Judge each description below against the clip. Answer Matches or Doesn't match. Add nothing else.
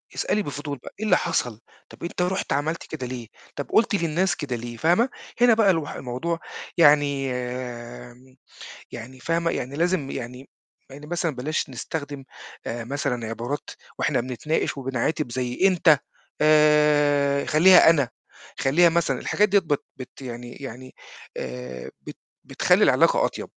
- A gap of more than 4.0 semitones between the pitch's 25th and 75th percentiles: Matches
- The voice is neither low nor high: Matches